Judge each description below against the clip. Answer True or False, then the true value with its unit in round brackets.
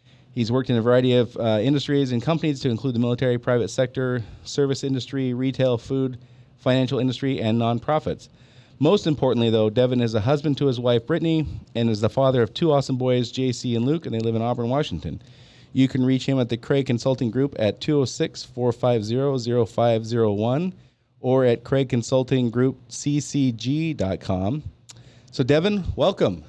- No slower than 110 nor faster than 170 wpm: True (165 wpm)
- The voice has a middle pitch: False (125 Hz)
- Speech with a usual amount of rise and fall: False (2.3 semitones)